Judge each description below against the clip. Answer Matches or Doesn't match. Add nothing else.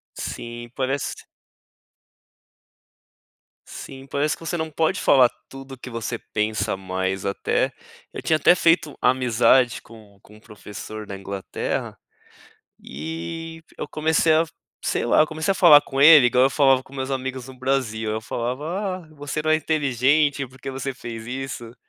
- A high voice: Doesn't match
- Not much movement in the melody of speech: Doesn't match